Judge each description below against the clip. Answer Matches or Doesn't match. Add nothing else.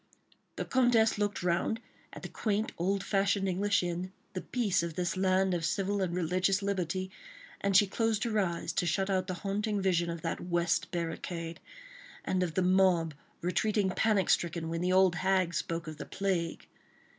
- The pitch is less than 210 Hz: Matches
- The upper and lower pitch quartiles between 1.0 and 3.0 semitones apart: Matches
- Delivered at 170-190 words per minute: Matches